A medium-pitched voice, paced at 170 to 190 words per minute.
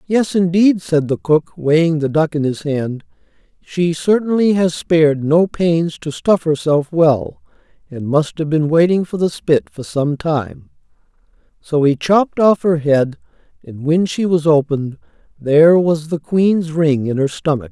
Yes: medium, 160 Hz; average, 175 wpm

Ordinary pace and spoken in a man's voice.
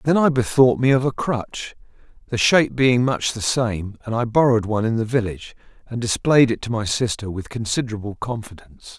Yes: average, 195 wpm; male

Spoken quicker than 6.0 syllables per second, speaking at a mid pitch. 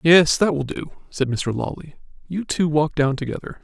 No: 4.9 syllables/s; medium, 155 Hz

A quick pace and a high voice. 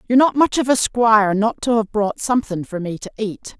Yes: fast, 250 wpm; high, 220 Hz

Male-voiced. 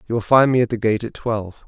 Yes: male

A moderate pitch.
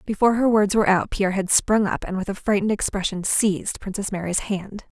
No: high, 200 Hz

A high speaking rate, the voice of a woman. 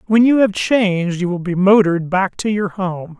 No: fast, 225 wpm; male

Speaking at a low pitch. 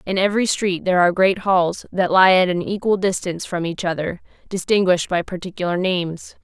No: medium, 185 Hz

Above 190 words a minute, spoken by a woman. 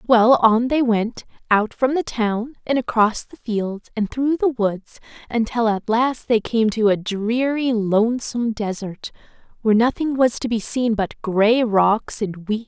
No: average, 185 wpm; female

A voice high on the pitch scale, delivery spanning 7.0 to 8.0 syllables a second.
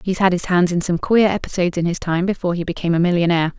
No: medium, 180 Hz; 7.5 syllables/s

